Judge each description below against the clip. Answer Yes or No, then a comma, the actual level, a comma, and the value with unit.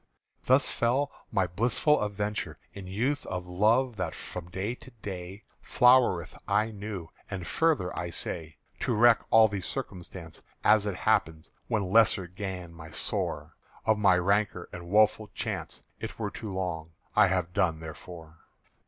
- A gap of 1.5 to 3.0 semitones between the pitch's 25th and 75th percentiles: No, average, 3.8 semitones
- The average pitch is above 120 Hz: No, low, 100 Hz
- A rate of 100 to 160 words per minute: Yes, average, 155 wpm